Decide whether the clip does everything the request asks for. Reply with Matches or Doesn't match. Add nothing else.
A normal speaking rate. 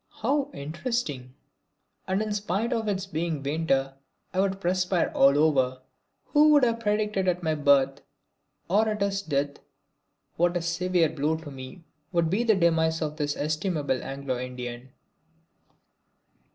Matches